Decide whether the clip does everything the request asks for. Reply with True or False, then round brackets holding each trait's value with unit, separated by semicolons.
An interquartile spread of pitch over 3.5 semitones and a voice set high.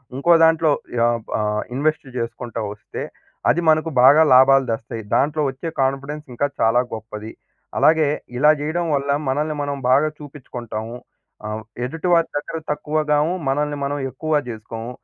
False (4.4 semitones; 140 Hz)